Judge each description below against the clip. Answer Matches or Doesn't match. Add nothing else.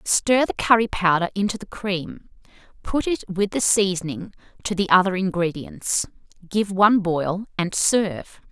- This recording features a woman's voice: Matches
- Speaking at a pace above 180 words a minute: Doesn't match